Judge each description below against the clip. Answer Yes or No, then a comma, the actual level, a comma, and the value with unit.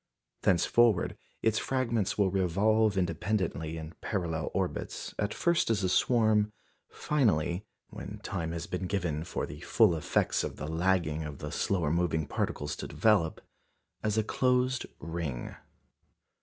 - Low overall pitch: Yes, very low, 95 Hz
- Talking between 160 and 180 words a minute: No, average, 140 wpm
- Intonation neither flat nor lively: Yes, average, 5.0 semitones